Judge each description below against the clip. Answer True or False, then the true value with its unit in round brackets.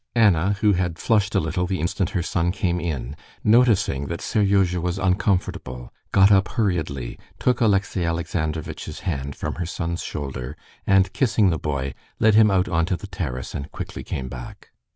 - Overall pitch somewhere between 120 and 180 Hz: False (90 Hz)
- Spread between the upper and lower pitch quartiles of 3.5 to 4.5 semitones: True (4.1 semitones)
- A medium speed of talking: True (170 wpm)